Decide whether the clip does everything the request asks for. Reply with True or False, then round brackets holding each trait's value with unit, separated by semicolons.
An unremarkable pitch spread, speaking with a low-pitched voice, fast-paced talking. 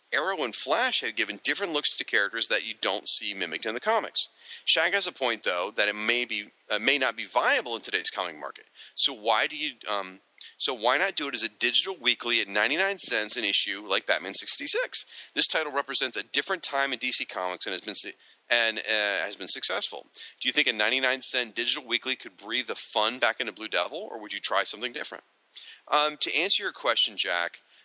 False (5.9 semitones; 125 Hz; 220 wpm)